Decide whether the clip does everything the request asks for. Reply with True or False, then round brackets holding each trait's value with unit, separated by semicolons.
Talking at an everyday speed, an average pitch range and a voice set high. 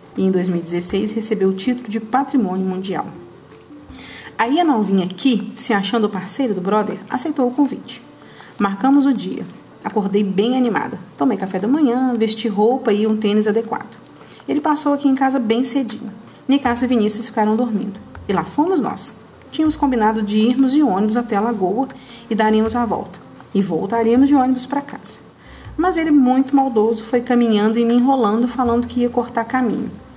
True (175 wpm; 3.6 semitones; 235 Hz)